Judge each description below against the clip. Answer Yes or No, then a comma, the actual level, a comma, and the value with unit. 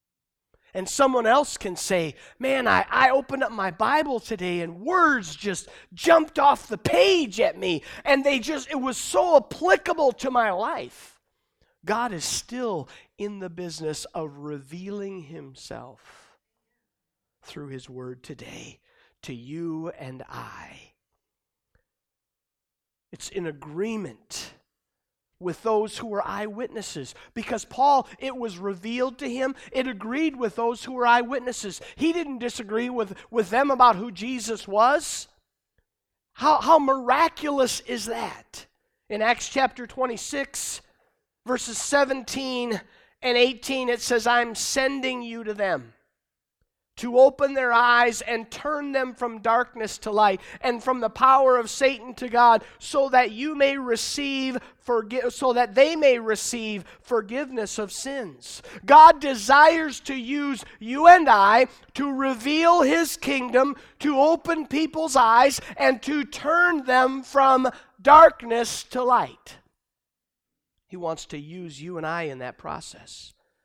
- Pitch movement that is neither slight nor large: Yes, average, 4.2 semitones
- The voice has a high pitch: Yes, high, 245 Hz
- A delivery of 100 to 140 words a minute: Yes, slow, 135 wpm